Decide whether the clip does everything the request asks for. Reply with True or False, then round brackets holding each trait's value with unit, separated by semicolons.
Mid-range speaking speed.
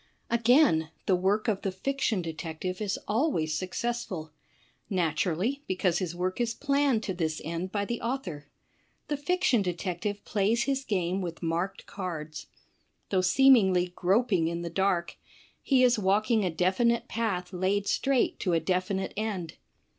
True (150 wpm)